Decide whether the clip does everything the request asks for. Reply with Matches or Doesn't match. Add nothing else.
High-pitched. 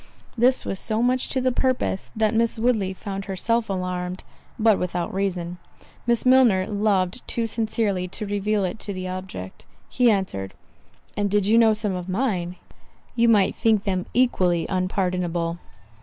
Matches